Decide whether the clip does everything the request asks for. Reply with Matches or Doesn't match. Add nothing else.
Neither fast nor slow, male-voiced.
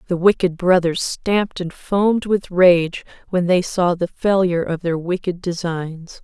Doesn't match